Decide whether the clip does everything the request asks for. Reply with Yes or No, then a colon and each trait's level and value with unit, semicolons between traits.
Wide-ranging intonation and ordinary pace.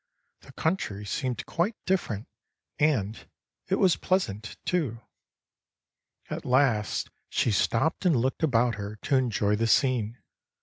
No: wide, 6.5 semitones; slow, 125 wpm